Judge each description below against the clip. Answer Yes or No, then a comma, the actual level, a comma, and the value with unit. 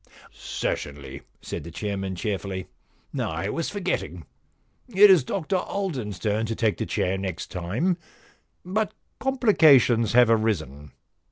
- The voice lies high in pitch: No, low, 110 Hz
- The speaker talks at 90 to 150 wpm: Yes, slow, 135 wpm